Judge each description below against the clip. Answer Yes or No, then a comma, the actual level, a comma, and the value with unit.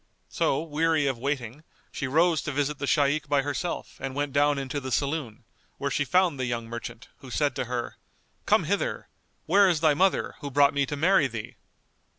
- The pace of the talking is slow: No, average, 195 wpm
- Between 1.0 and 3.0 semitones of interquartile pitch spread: Yes, narrow, 2.6 semitones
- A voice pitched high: No, medium, 140 Hz